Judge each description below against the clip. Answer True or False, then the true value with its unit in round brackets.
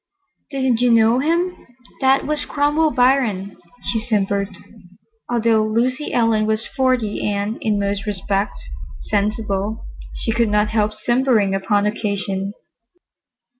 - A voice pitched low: False (220 Hz)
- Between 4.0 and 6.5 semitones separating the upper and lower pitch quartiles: False (3.6 semitones)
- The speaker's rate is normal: False (120 wpm)